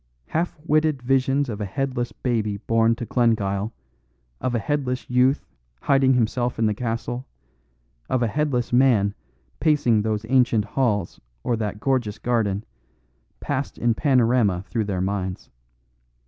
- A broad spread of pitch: No, average, 3.6 semitones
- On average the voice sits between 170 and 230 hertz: No, low, 120 Hz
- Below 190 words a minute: Yes, slow, 135 wpm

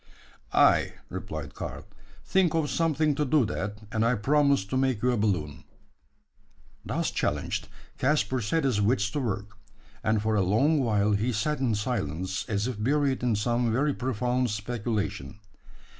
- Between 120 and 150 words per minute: No, average, 160 wpm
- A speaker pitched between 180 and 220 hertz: No, low, 115 Hz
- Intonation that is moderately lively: Yes, average, 4.4 semitones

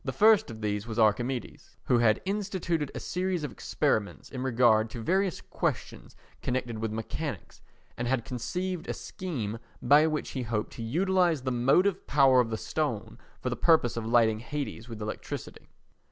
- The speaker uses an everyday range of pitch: No, wide, 6.2 semitones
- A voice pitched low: Yes, low, 125 Hz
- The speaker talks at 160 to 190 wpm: Yes, average, 170 wpm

